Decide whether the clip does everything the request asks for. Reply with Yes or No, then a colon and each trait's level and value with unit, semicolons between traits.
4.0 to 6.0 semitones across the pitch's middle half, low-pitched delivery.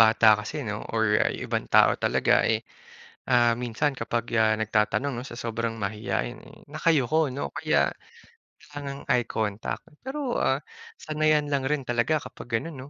Yes: average, 4.8 semitones; low, 125 Hz